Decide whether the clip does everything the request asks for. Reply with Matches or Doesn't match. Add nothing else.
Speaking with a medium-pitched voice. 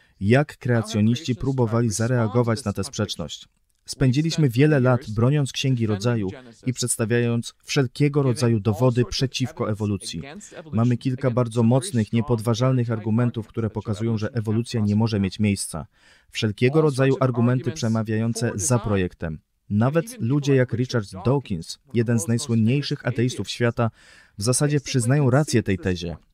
Doesn't match